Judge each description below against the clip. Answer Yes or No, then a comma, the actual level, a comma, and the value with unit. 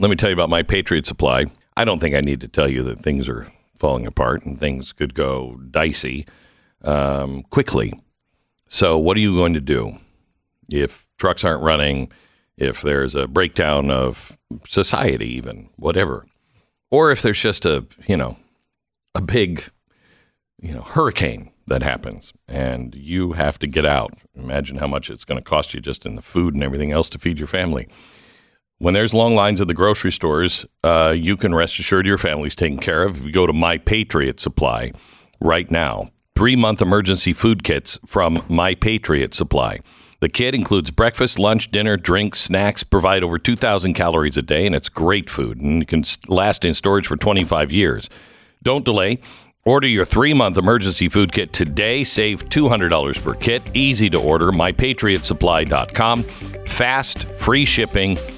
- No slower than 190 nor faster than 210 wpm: No, average, 175 wpm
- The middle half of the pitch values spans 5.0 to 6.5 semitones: Yes, wide, 5.6 semitones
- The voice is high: No, very low, 90 Hz